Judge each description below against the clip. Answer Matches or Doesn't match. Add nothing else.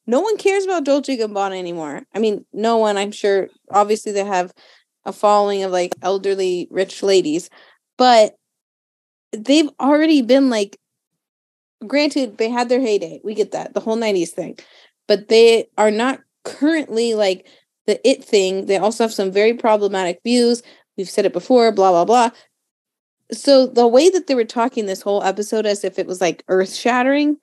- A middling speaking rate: Matches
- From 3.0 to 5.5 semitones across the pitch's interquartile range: Matches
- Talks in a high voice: Matches